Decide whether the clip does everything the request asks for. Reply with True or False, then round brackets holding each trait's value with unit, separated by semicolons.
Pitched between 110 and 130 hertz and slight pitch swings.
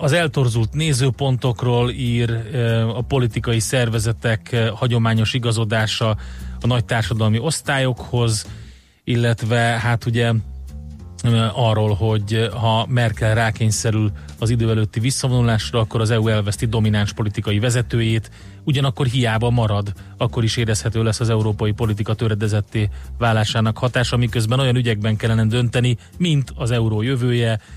True (115 Hz; 1.9 semitones)